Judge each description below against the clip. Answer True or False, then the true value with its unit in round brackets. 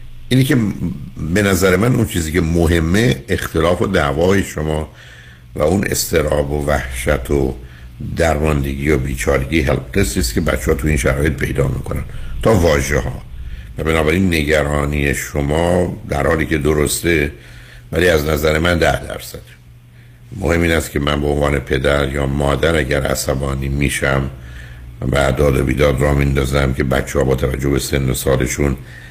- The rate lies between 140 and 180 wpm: True (155 wpm)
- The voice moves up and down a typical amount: True (3.7 semitones)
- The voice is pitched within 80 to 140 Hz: False (70 Hz)